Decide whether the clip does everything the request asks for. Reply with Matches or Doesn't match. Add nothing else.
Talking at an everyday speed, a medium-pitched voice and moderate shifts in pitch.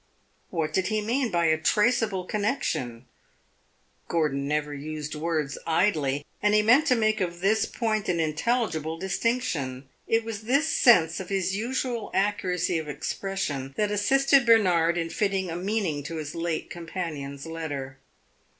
Doesn't match